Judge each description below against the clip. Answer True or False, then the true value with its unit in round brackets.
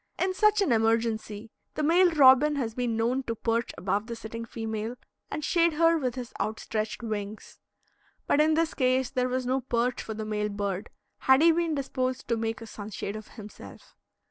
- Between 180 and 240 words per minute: True (190 wpm)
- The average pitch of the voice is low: False (240 Hz)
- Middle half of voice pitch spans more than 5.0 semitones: False (4.3 semitones)